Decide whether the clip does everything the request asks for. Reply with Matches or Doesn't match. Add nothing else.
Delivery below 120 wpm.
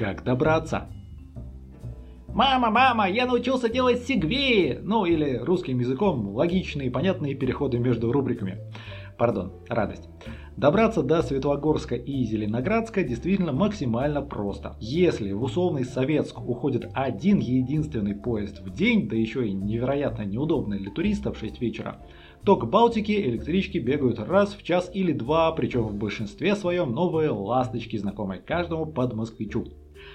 Doesn't match